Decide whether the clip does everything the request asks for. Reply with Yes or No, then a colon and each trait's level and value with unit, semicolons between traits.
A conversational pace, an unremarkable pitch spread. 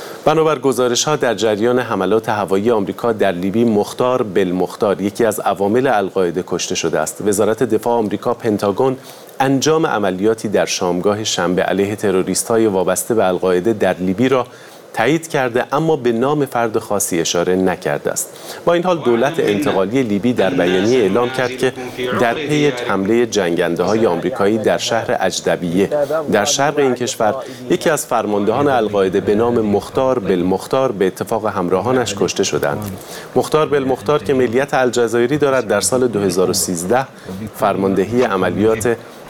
Yes: average, 145 wpm; average, 5.0 semitones